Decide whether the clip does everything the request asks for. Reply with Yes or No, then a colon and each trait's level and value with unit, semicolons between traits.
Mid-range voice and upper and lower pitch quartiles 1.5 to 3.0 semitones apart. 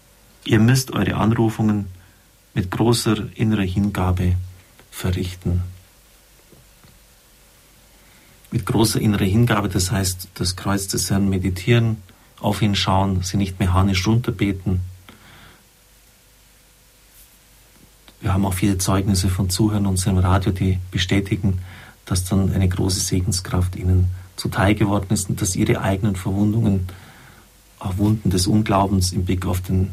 No: low, 100 Hz; narrow, 2.5 semitones